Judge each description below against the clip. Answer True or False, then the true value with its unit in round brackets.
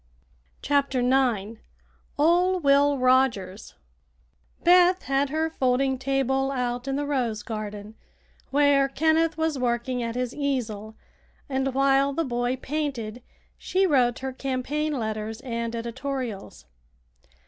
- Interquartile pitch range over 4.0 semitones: False (3.0 semitones)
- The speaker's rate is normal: False (115 wpm)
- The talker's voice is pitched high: True (265 Hz)